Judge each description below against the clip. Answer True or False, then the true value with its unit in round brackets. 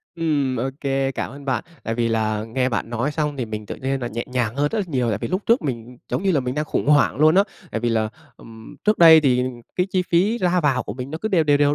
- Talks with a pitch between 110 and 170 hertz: True (135 Hz)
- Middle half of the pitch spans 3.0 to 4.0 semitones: False (4.9 semitones)